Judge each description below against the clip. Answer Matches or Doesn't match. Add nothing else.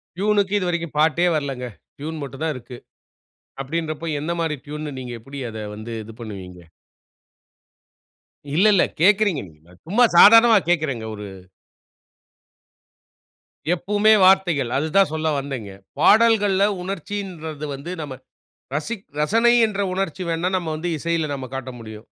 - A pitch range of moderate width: Doesn't match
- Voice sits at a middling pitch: Matches